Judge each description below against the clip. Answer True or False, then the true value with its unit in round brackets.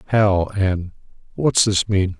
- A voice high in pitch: False (95 Hz)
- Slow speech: True (110 wpm)